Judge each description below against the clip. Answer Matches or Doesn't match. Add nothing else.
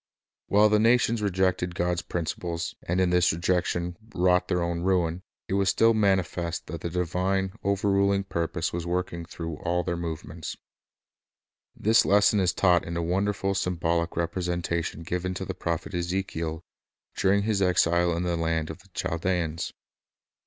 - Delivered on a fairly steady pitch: Matches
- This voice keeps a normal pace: Matches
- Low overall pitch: Matches